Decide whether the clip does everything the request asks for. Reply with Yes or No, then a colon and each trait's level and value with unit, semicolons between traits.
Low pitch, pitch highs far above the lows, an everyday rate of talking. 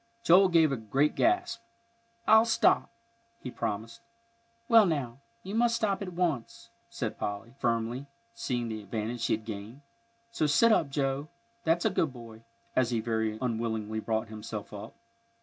Yes: low, 125 Hz; wide, 7.7 semitones; average, 155 wpm